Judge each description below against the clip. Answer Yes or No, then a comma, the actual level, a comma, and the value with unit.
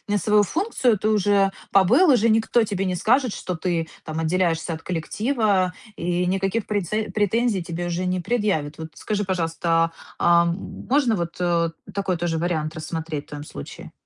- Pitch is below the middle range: No, medium, 185 Hz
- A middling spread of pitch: Yes, average, 4.2 semitones